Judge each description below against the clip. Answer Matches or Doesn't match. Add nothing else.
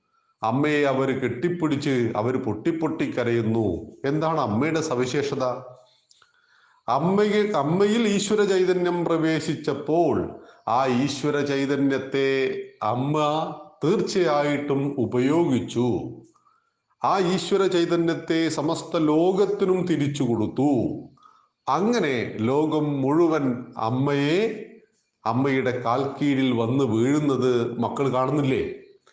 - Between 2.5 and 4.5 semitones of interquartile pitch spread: Doesn't match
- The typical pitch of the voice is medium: Matches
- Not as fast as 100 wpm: Matches